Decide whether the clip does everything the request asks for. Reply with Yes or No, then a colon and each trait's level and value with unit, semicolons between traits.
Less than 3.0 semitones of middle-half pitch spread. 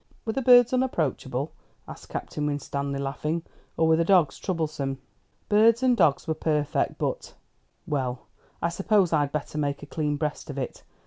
No: average, 4.7 semitones